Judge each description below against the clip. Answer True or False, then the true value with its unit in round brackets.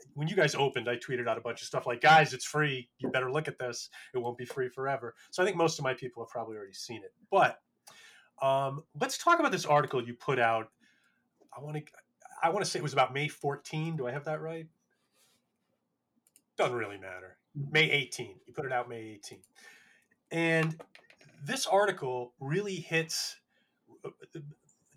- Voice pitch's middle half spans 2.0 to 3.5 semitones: False (4.4 semitones)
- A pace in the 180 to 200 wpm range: True (195 wpm)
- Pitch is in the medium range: True (145 Hz)